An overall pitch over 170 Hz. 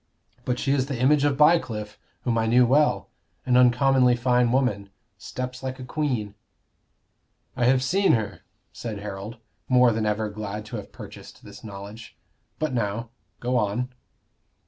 No: low, 125 Hz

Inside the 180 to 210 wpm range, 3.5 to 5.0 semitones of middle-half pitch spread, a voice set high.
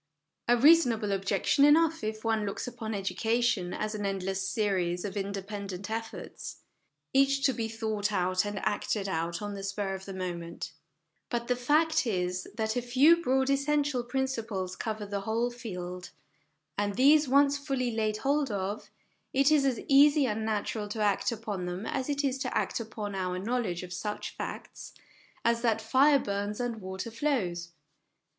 No: average, 170 wpm; average, 4.7 semitones; high, 220 Hz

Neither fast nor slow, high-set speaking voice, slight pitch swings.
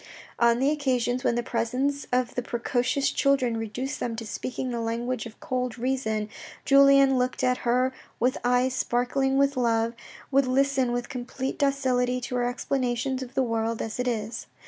Yes: average, 170 wpm; very high, 250 Hz; narrow, 2.0 semitones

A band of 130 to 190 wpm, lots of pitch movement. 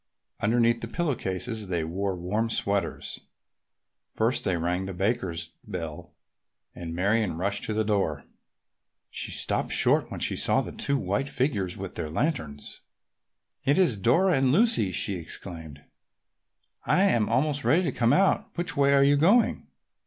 Yes: average, 155 wpm; wide, 7.3 semitones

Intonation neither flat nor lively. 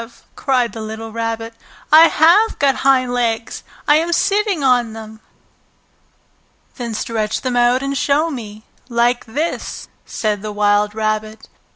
Yes: average, 4.0 semitones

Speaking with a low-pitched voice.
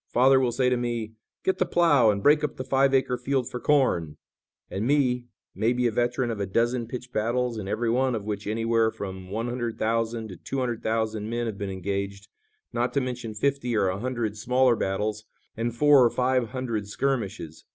Yes: low, 120 Hz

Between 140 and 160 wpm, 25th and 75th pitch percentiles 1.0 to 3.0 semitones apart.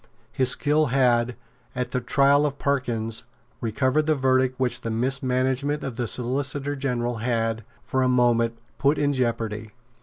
Yes: average, 150 wpm; average, 2.7 semitones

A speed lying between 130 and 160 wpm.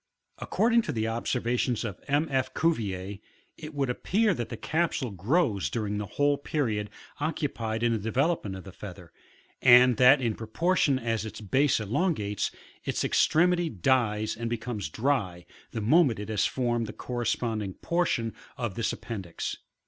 Yes: average, 155 wpm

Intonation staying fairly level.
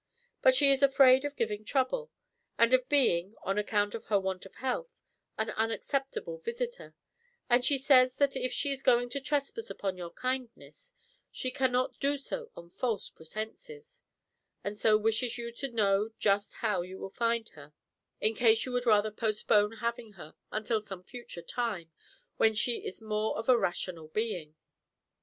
No: average, 4.2 semitones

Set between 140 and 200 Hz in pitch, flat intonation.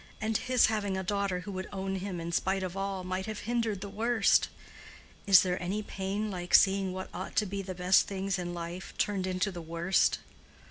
Yes: high, 190 Hz; narrow, 1.7 semitones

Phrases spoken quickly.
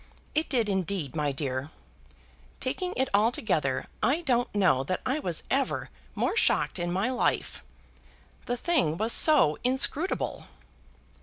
No: slow, 135 wpm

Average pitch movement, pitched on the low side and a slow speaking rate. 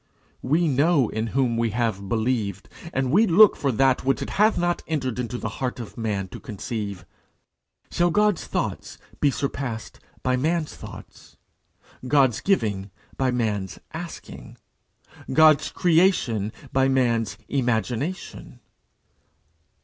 No: wide, 5.7 semitones; low, 130 Hz; slow, 125 wpm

